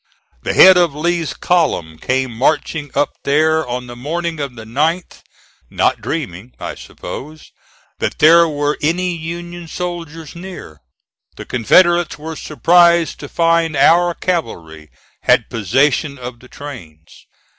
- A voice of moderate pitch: Yes, medium, 155 Hz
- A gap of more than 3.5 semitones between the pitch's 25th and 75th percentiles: Yes, average, 5.1 semitones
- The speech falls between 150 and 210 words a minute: No, slow, 135 wpm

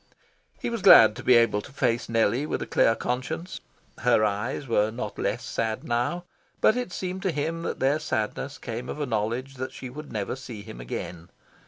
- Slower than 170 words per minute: No, average, 200 wpm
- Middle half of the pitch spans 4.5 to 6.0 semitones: Yes, average, 5.1 semitones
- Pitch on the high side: No, low, 125 Hz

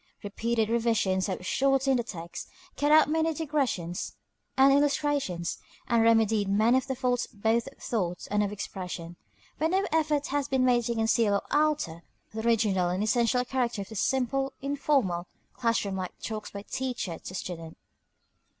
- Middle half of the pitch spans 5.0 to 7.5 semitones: Yes, average, 5.3 semitones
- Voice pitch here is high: Yes, high, 235 Hz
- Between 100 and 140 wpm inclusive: No, average, 160 wpm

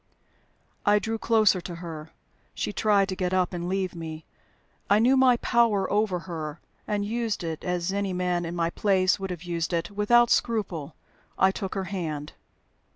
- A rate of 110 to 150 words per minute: No, average, 175 wpm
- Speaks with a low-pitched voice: No, medium, 185 Hz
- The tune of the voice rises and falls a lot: No, average, 3.3 semitones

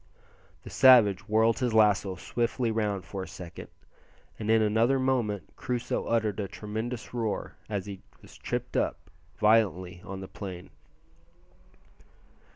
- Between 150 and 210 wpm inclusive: No, slow, 135 wpm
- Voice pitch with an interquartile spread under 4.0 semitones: Yes, average, 2.8 semitones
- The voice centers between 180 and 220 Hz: No, low, 105 Hz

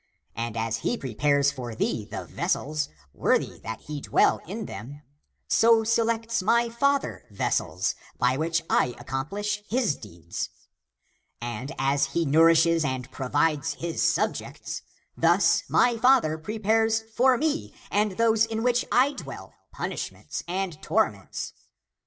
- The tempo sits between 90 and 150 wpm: Yes, average, 140 wpm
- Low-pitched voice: No, medium, 165 Hz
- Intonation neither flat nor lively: No, wide, 8.8 semitones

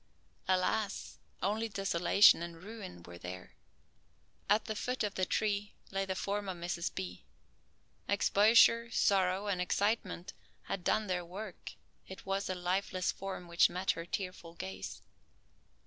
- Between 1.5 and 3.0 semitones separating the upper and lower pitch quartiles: Yes, narrow, 2.6 semitones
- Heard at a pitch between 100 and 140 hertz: No, high, 190 Hz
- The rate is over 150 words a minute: No, average, 140 wpm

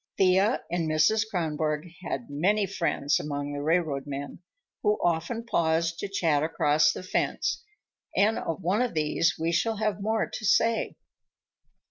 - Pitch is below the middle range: No, medium, 170 Hz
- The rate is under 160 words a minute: Yes, average, 150 wpm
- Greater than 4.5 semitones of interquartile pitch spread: Yes, average, 5.0 semitones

